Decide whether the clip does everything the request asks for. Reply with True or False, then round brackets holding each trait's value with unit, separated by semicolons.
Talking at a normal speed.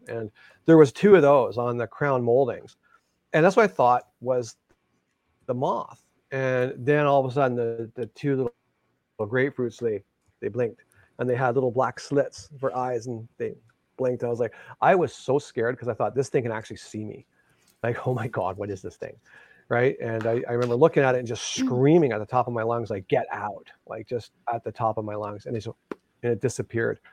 False (230 wpm)